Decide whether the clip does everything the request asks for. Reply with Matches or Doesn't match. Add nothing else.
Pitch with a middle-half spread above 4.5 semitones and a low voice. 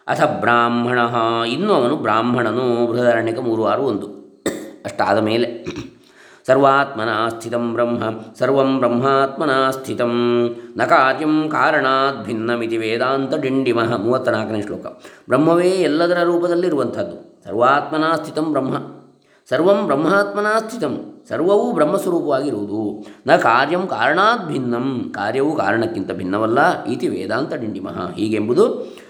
Matches